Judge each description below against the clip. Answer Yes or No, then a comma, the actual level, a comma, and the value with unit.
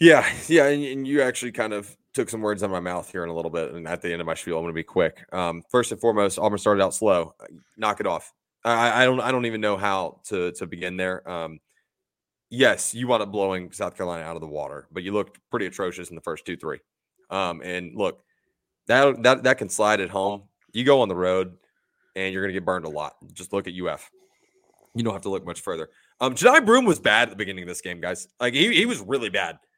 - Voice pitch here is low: Yes, low, 100 Hz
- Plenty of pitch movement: Yes, wide, 6.2 semitones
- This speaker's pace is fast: Yes, fast, 260 wpm